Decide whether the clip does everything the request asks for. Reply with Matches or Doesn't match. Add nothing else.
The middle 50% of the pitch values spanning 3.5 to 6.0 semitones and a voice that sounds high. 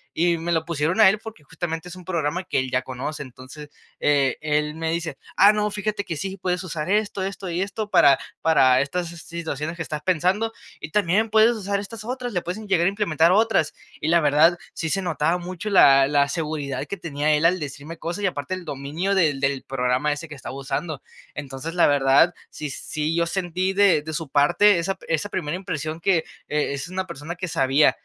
Doesn't match